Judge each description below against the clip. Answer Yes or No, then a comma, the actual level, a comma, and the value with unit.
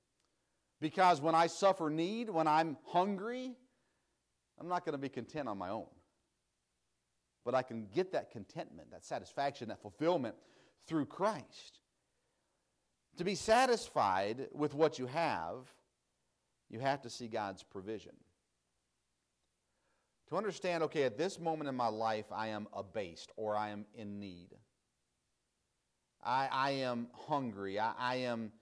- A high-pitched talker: No, low, 125 Hz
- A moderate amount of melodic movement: No, wide, 8.7 semitones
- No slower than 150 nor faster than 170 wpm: No, average, 140 wpm